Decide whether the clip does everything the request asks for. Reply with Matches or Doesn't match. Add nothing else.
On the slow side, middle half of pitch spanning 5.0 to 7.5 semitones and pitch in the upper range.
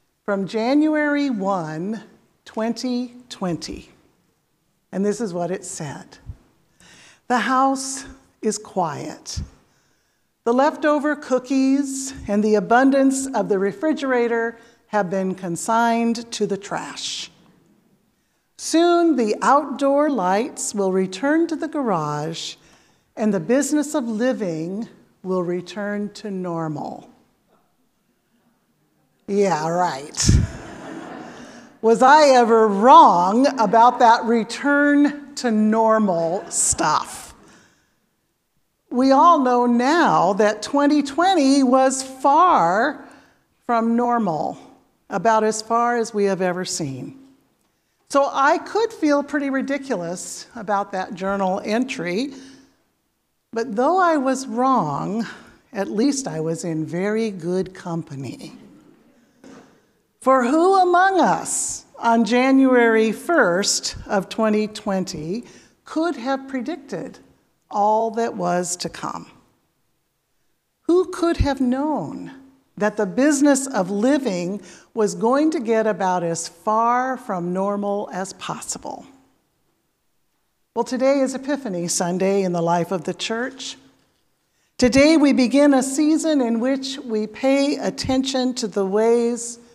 Matches